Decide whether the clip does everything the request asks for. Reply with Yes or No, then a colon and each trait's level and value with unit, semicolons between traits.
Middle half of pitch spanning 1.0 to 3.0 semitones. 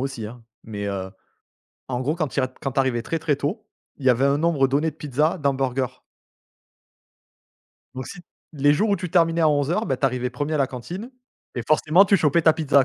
No: average, 3.6 semitones